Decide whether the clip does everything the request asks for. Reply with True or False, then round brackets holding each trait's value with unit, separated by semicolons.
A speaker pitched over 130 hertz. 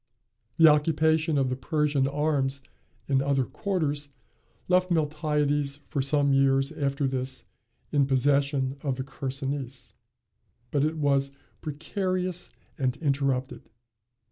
True (140 Hz)